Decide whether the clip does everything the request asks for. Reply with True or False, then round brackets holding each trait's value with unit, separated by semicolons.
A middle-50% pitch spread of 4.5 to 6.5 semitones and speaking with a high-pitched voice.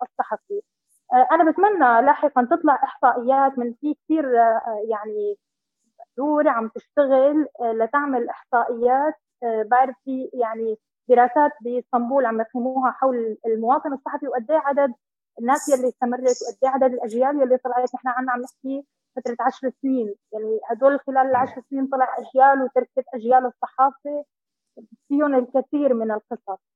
False (2.4 semitones; 255 Hz)